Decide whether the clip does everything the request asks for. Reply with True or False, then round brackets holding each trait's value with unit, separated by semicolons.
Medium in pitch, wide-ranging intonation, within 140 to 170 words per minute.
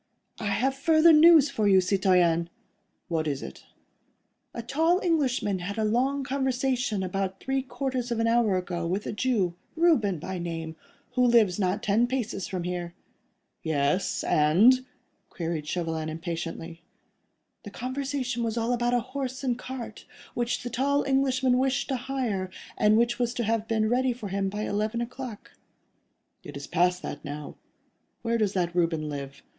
False (220 Hz; 6.1 semitones; 160 wpm)